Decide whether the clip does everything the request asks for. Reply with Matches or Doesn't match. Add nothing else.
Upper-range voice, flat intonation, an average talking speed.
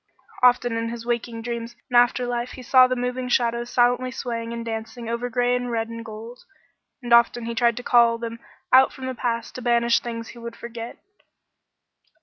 Matches